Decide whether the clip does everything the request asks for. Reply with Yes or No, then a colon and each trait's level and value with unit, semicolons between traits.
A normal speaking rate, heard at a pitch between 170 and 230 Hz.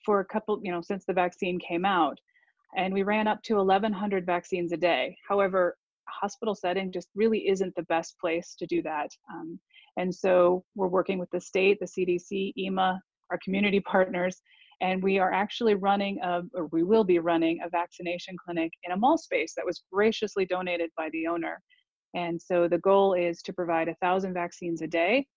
Yes: average, 195 wpm; medium, 185 Hz